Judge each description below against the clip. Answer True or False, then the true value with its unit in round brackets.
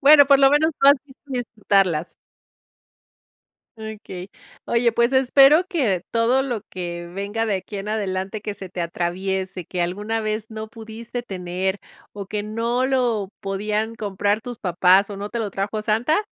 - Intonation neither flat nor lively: True (3.6 semitones)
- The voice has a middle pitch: False (215 Hz)